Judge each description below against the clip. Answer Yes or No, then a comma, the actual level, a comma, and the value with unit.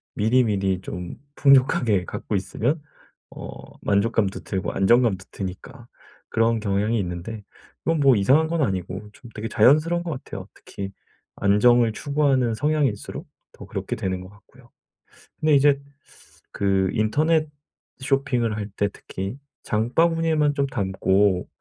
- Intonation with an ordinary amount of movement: No, wide, 5.9 semitones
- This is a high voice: No, low, 115 Hz